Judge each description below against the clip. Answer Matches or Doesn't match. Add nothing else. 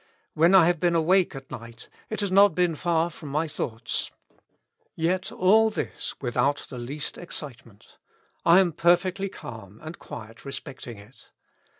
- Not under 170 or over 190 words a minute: Doesn't match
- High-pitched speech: Doesn't match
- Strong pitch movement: Matches